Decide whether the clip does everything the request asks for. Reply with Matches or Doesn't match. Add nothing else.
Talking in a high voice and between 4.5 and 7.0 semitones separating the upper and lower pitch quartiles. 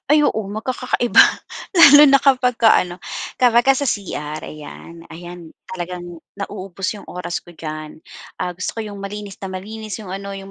Matches